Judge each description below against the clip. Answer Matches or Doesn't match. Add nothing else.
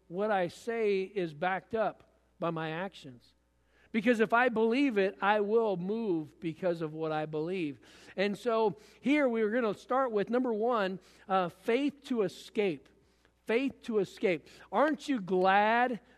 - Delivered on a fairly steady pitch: Doesn't match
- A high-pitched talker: Matches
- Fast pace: Doesn't match